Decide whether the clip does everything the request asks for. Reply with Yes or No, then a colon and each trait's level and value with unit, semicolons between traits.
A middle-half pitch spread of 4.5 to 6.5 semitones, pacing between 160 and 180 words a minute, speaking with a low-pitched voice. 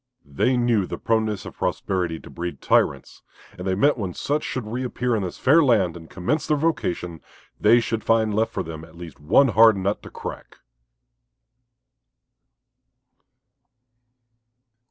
No: wide, 5.4 semitones; average, 150 wpm; low, 110 Hz